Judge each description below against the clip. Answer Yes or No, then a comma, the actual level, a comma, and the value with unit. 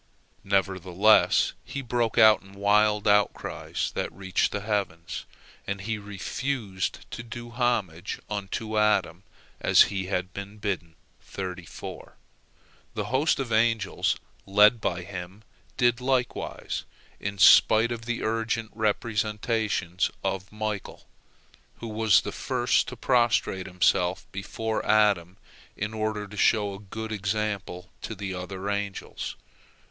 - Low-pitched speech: Yes, low, 105 Hz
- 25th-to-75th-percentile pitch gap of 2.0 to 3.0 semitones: Yes, narrow, 2.5 semitones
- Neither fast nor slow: No, slow, 120 wpm